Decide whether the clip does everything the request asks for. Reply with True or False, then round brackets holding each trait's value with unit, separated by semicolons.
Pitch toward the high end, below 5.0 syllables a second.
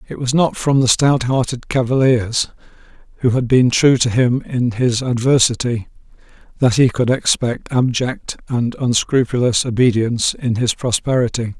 False (125 Hz; 4.6 syllables/s)